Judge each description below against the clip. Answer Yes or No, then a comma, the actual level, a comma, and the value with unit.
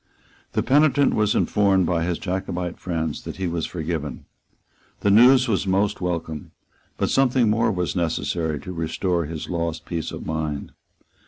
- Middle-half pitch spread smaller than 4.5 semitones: Yes, average, 3.7 semitones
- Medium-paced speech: Yes, average, 155 wpm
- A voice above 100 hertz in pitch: No, very low, 90 Hz